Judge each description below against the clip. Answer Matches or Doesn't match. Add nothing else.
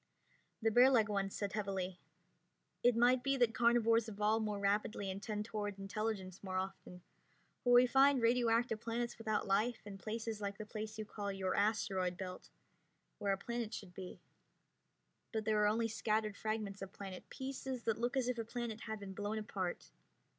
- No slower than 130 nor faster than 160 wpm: Doesn't match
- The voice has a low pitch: Doesn't match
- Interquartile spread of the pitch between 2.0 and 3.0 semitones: Matches